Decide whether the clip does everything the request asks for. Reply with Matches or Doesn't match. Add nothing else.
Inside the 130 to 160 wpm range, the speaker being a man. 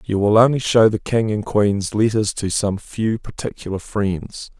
Doesn't match